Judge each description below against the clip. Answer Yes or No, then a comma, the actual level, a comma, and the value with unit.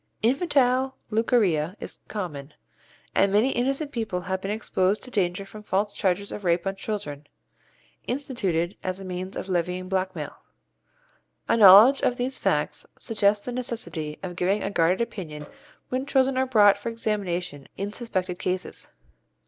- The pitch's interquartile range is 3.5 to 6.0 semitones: Yes, average, 4.4 semitones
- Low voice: No, high, 200 Hz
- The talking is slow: No, average, 150 wpm